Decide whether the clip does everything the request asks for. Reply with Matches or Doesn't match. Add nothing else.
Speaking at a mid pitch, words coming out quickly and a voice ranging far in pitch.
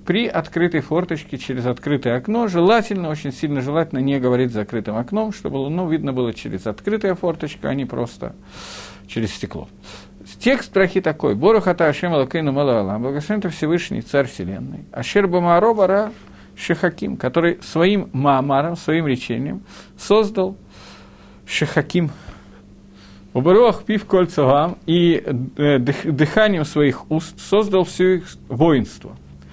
Doesn't match